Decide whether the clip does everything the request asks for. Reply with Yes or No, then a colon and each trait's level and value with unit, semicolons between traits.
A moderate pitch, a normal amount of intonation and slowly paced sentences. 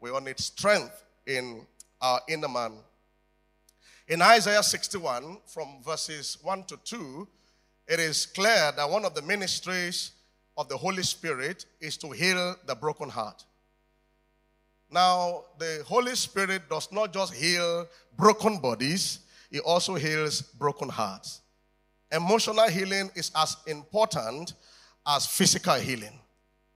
Yes: medium, 165 Hz; average, 4.4 semitones; slow, 130 wpm